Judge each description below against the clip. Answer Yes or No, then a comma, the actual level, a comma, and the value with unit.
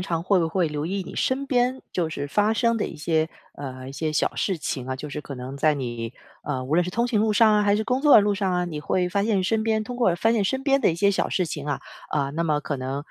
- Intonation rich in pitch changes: Yes, wide, 6.5 semitones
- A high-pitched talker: No, medium, 180 Hz